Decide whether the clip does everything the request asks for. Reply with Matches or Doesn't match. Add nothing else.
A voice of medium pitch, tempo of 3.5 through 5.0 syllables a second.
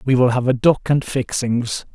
Doesn't match